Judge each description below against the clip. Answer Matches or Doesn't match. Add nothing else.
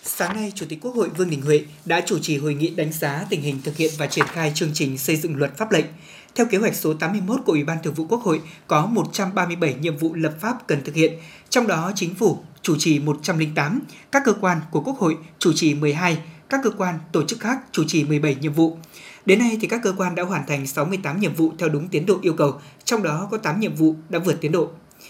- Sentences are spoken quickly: Matches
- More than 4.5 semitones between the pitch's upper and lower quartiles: Doesn't match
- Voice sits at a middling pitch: Matches